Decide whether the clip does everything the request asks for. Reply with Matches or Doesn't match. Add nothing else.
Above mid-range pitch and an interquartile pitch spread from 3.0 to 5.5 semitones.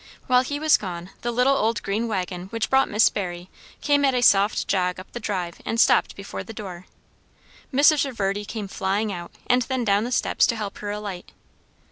Matches